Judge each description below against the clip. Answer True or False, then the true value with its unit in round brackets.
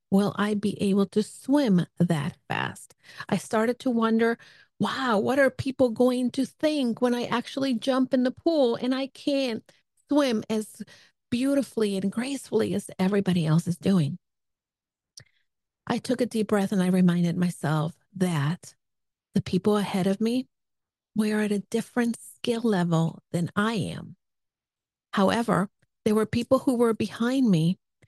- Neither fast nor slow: True (150 wpm)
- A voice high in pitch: True (215 Hz)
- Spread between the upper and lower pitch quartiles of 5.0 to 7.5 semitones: True (5.3 semitones)